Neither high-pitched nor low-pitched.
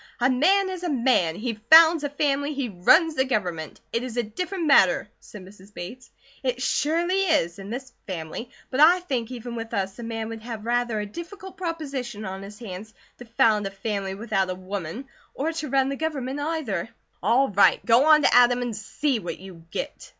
No: high, 240 Hz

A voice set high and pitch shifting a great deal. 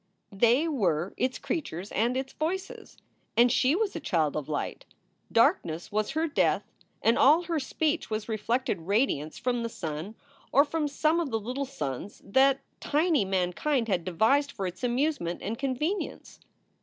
Yes: high, 245 Hz; wide, 7.0 semitones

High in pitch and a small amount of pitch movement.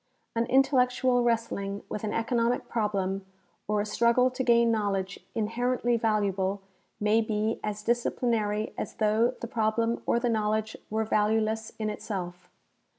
Yes: high, 220 Hz; narrow, 2.0 semitones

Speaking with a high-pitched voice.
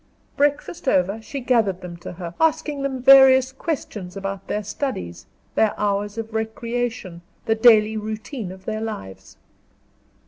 Yes: high, 220 Hz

